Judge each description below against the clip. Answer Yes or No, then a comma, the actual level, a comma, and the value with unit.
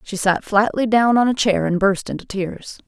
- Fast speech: Yes, fast, 230 wpm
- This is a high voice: Yes, high, 205 Hz